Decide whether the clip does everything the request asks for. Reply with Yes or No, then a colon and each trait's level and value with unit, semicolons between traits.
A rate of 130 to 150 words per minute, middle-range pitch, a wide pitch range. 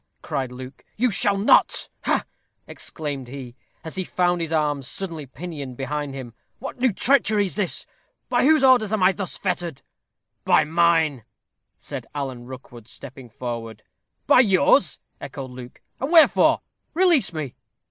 Yes: average, 145 wpm; medium, 160 Hz; wide, 7.3 semitones